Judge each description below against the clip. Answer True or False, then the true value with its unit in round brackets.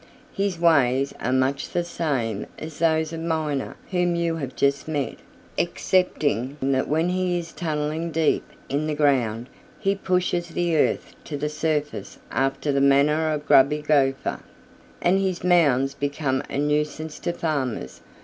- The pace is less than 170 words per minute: True (150 wpm)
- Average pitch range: True (3.4 semitones)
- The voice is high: False (150 Hz)